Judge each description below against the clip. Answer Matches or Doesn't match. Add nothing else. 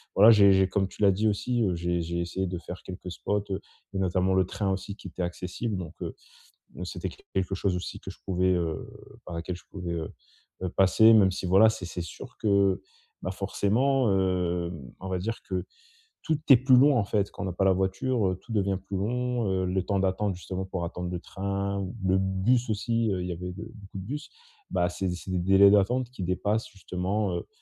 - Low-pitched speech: Matches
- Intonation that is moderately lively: Doesn't match